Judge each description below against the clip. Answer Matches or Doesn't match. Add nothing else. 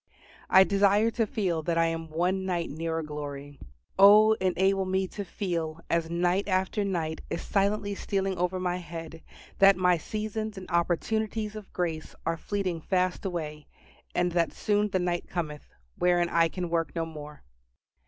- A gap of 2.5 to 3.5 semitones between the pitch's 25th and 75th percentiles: Matches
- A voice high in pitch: Doesn't match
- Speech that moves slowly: Doesn't match